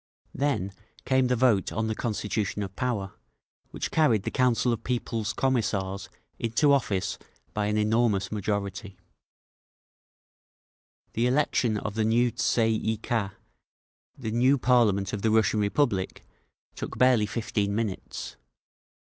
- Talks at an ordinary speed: No, slow, 130 wpm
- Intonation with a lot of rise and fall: No, average, 3.2 semitones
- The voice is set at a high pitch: No, low, 110 Hz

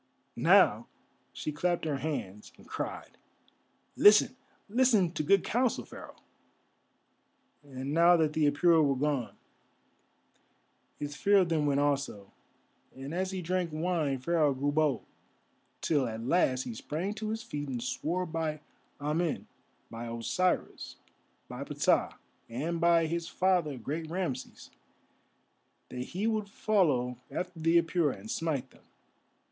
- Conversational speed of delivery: No, slow, 130 wpm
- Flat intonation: No, average, 4.4 semitones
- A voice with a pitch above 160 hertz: No, medium, 155 Hz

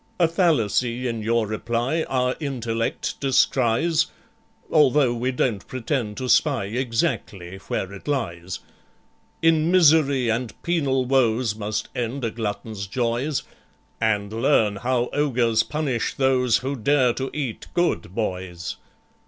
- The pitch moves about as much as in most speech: Yes, average, 3.7 semitones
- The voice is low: Yes, low, 125 Hz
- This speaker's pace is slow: Yes, slow, 125 wpm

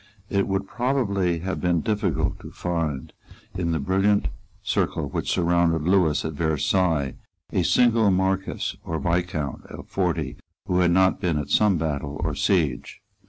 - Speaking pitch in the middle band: No, very low, 90 Hz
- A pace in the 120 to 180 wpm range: Yes, average, 150 wpm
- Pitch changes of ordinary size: Yes, average, 3.5 semitones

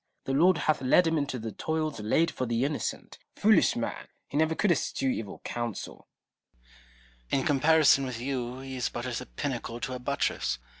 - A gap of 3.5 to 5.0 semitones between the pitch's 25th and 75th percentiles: Yes, average, 4.1 semitones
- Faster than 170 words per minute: Yes, average, 190 wpm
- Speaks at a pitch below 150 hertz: Yes, low, 135 Hz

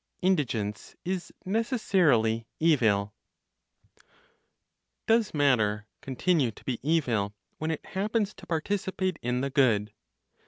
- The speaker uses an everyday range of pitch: No, wide, 8.7 semitones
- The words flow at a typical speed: No, slow, 105 wpm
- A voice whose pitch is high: No, medium, 145 Hz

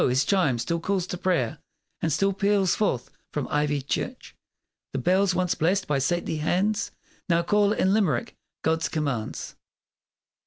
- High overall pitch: No, medium, 175 Hz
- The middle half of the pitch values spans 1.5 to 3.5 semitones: No, average, 4.9 semitones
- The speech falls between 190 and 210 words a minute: No, average, 150 wpm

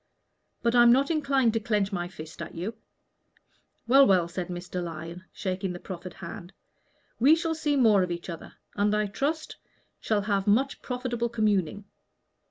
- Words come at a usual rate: Yes, average, 165 wpm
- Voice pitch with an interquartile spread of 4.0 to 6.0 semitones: Yes, average, 5.3 semitones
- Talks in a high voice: Yes, high, 205 Hz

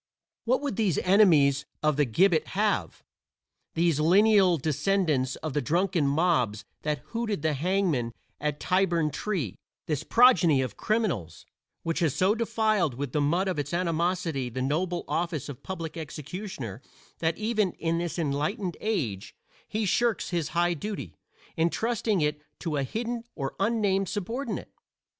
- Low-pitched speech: No, medium, 170 Hz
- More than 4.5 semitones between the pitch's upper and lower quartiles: Yes, average, 5.2 semitones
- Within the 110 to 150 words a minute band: Yes, average, 145 wpm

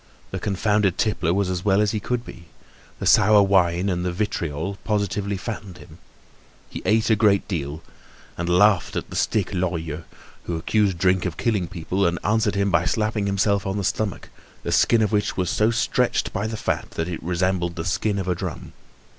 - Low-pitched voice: Yes, very low, 95 Hz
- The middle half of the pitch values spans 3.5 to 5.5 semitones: No, average, 3.1 semitones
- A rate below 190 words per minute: No, average, 195 wpm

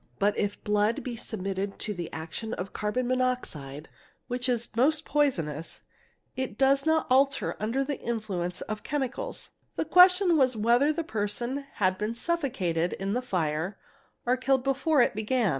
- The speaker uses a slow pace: No, average, 160 wpm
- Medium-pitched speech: No, high, 235 Hz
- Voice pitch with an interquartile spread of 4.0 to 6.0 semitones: Yes, average, 5.3 semitones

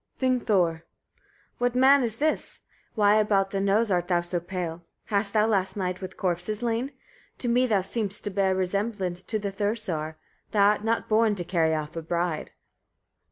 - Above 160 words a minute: Yes, average, 180 wpm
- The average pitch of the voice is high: Yes, high, 200 Hz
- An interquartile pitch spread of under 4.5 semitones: Yes, average, 3.7 semitones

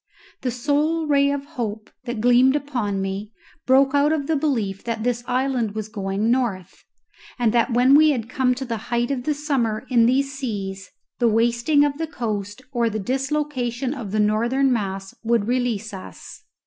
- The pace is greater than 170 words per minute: Yes, average, 180 wpm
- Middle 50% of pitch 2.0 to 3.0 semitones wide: No, average, 4.1 semitones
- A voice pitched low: No, high, 240 Hz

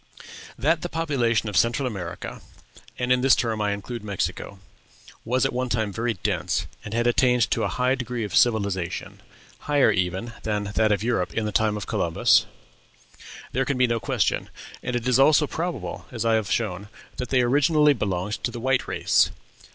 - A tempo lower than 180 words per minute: No, average, 185 wpm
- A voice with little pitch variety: No, average, 3.6 semitones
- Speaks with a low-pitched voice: Yes, low, 115 Hz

